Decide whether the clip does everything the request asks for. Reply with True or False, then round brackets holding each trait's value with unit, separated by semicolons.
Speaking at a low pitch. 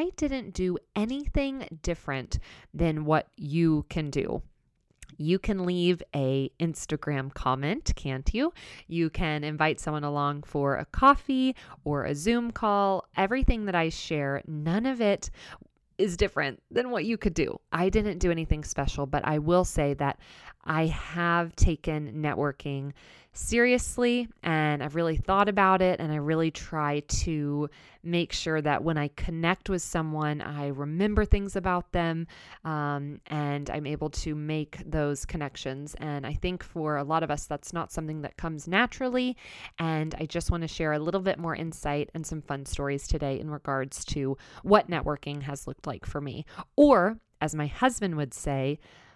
False (160 Hz)